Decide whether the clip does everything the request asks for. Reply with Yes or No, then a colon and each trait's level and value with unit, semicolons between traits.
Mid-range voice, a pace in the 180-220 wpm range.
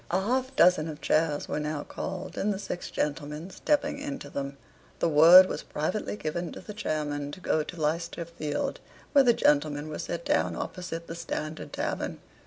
Yes: medium, 165 Hz; average, 185 wpm